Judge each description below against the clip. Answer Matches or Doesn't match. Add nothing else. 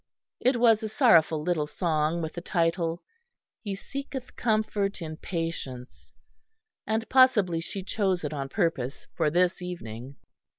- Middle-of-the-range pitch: Matches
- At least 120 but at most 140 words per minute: Matches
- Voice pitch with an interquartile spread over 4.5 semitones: Matches